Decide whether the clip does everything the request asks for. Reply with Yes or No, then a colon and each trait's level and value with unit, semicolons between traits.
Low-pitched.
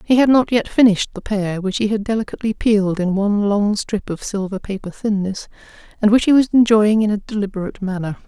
No: high, 205 Hz